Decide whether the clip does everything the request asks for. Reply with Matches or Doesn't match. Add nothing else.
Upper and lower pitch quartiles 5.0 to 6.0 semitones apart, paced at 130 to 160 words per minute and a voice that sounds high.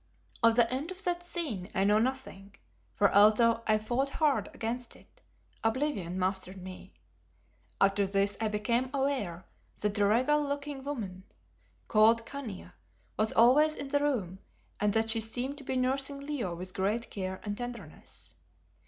Matches